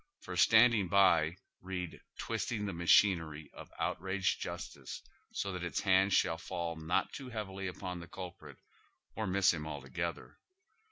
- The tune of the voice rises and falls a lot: No, narrow, 2.6 semitones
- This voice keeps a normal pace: Yes, average, 150 wpm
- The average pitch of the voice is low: Yes, very low, 90 Hz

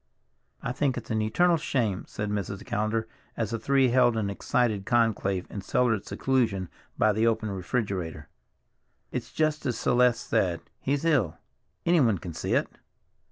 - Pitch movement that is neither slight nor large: Yes, average, 4.0 semitones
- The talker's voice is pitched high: No, low, 110 Hz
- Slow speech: No, average, 150 wpm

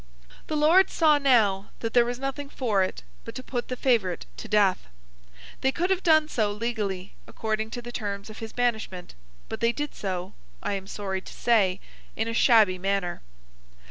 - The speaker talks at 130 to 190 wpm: Yes, average, 185 wpm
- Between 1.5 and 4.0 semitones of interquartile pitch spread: No, average, 4.6 semitones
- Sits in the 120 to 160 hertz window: No, high, 225 Hz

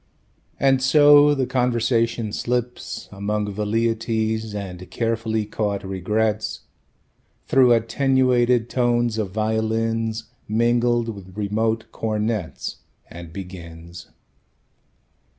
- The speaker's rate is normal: No, slow, 85 wpm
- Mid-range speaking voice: No, low, 110 Hz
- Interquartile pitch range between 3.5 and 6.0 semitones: No, narrow, 2.5 semitones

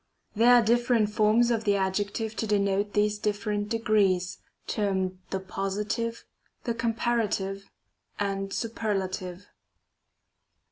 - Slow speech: Yes, slow, 110 wpm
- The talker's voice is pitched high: Yes, high, 210 Hz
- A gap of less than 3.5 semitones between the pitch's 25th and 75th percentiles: Yes, narrow, 2.4 semitones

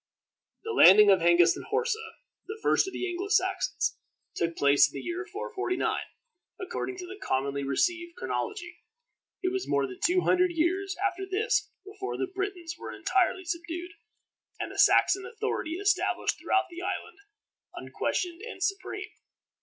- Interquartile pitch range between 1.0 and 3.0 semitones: Yes, narrow, 2.5 semitones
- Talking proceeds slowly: No, average, 155 wpm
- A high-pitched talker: Yes, very high, 365 Hz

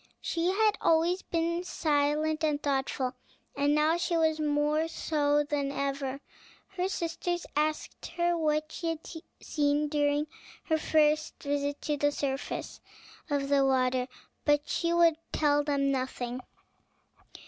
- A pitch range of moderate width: No, narrow, 2.3 semitones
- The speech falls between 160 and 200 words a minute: No, slow, 135 wpm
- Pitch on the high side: Yes, very high, 300 Hz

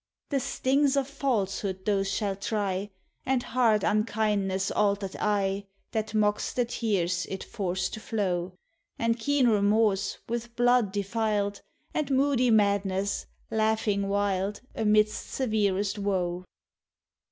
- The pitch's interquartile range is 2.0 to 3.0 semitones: Yes, average, 2.7 semitones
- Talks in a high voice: Yes, high, 210 Hz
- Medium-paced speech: No, slow, 120 wpm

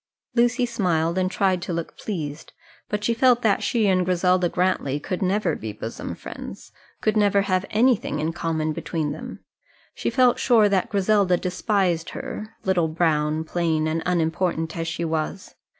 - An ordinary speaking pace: Yes, average, 165 wpm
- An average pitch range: Yes, average, 4.1 semitones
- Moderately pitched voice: Yes, medium, 180 Hz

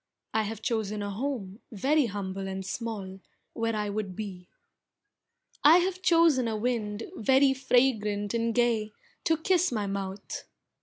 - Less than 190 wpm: Yes, average, 145 wpm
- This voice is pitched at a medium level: No, high, 220 Hz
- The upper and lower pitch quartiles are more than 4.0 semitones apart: Yes, average, 4.4 semitones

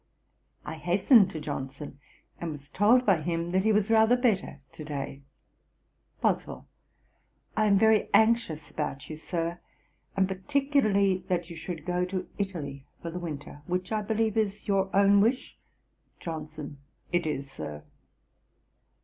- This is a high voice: No, medium, 180 Hz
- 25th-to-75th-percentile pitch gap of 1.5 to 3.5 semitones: No, average, 5.2 semitones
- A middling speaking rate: Yes, average, 145 wpm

